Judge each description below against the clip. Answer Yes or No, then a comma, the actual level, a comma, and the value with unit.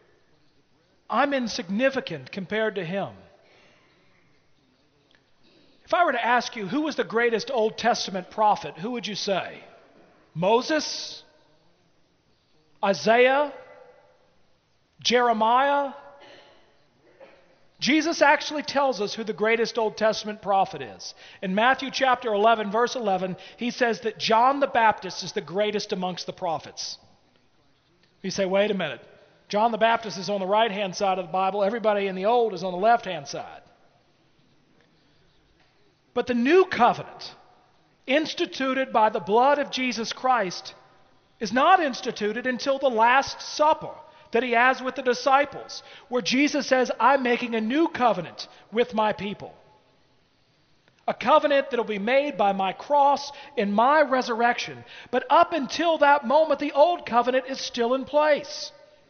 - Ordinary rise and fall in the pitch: Yes, average, 4.7 semitones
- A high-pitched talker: Yes, high, 235 Hz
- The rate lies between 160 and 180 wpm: No, average, 140 wpm